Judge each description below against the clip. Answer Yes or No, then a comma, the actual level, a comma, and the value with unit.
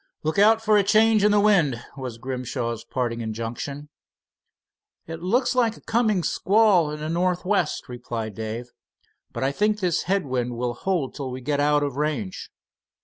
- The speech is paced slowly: No, average, 170 wpm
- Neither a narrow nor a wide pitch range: No, wide, 8.5 semitones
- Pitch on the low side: No, medium, 150 Hz